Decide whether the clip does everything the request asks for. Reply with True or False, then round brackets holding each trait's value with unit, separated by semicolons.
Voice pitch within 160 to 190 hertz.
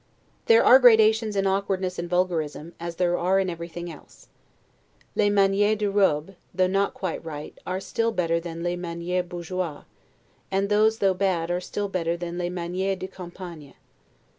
True (185 Hz)